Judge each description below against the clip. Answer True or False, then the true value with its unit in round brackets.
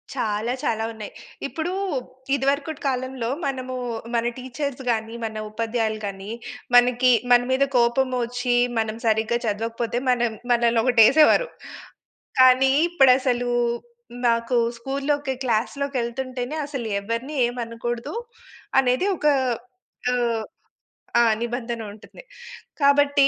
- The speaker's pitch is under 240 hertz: False (245 Hz)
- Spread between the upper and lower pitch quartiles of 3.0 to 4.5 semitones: False (2.6 semitones)